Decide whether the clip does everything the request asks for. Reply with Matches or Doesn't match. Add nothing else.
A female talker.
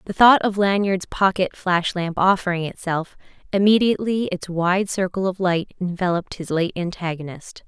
Matches